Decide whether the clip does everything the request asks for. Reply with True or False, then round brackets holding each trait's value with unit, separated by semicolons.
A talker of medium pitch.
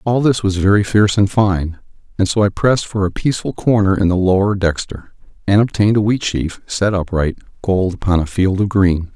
False (100 Hz)